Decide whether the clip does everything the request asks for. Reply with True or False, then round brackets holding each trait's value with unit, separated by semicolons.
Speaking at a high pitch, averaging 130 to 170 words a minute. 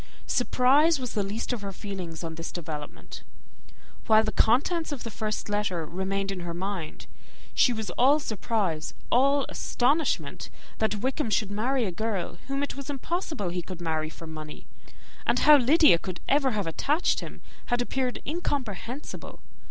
True (215 Hz; 165 wpm)